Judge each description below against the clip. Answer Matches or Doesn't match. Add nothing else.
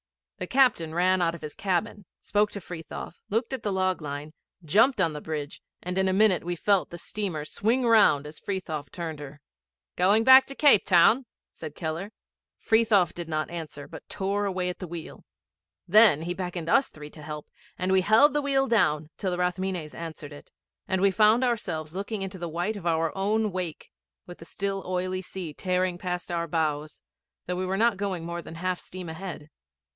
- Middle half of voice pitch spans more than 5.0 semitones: Doesn't match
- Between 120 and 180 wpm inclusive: Doesn't match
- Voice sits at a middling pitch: Matches